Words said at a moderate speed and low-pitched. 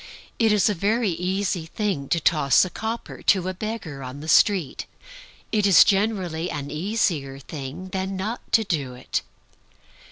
No: average, 160 wpm; medium, 185 Hz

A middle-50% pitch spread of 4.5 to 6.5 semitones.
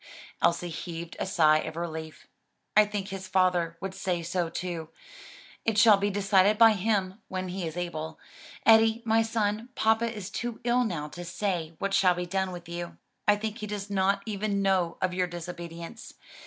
No: average, 3.3 semitones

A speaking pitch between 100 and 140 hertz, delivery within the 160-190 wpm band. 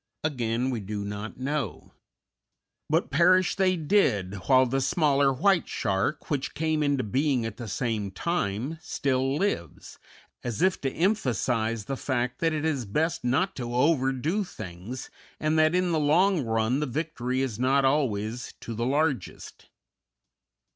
No: low, 135 Hz; average, 150 wpm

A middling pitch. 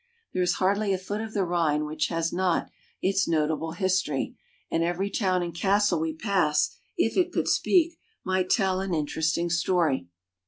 Yes: medium, 180 Hz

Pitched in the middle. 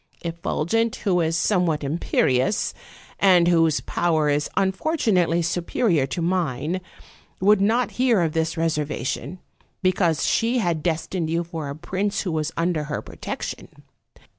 Yes: medium, 170 Hz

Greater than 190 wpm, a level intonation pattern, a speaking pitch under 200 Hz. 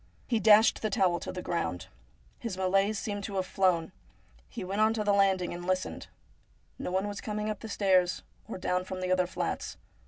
Yes: average, 200 wpm; narrow, 2.2 semitones; high, 190 Hz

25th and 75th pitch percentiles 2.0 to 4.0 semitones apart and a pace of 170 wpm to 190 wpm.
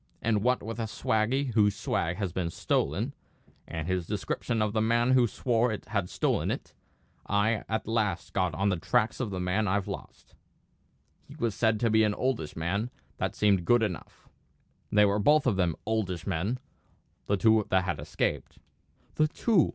Yes: average, 3.4 semitones; average, 180 wpm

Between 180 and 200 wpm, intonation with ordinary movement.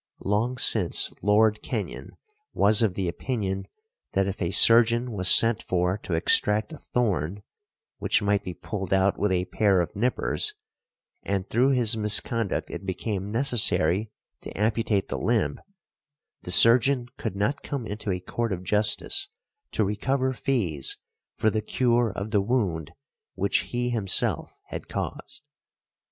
No: average, 145 wpm; average, 3.5 semitones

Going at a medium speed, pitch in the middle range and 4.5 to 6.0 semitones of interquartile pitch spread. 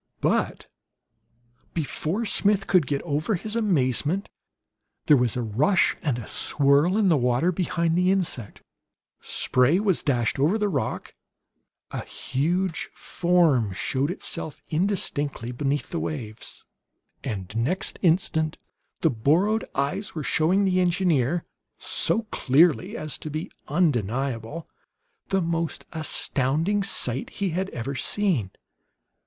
No: slow, 125 wpm; medium, 160 Hz; wide, 5.6 semitones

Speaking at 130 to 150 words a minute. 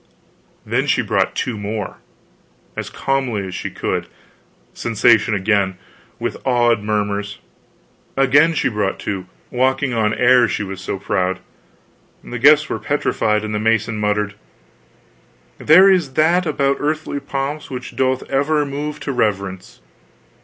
Yes: slow, 135 wpm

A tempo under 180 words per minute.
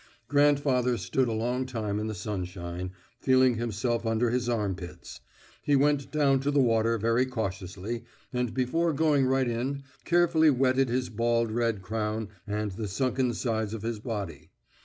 Yes: average, 160 wpm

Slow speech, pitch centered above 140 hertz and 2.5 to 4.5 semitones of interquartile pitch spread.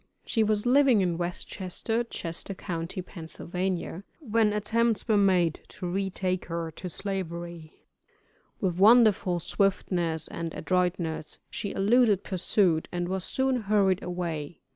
Yes: slow, 125 wpm; medium, 185 Hz; average, 3.5 semitones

